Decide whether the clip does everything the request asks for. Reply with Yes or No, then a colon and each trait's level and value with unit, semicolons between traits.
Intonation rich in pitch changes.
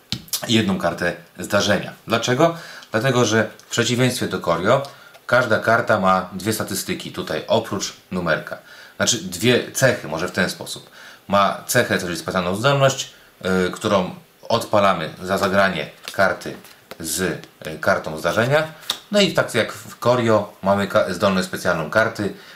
No: average, 4.8 semitones